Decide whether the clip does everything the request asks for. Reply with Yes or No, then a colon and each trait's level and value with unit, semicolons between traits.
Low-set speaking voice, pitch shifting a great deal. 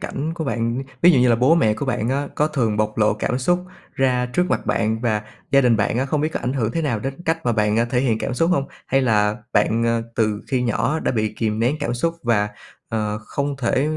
No: low, 125 Hz; average, 4.0 semitones